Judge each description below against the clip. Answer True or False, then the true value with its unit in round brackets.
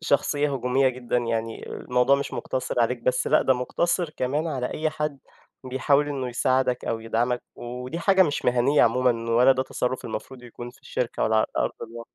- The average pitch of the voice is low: True (125 Hz)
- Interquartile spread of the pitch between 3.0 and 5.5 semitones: False (2.5 semitones)